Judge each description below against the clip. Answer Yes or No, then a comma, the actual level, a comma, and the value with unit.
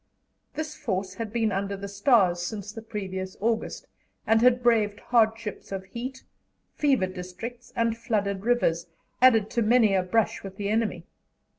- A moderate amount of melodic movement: Yes, average, 3.2 semitones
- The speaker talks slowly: No, average, 155 wpm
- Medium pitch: No, high, 215 Hz